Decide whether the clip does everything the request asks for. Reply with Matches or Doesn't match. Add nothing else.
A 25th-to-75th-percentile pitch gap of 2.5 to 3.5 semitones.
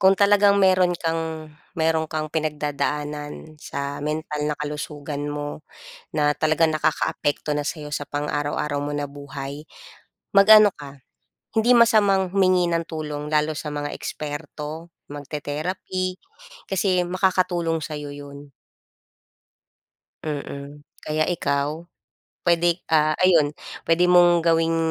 Matches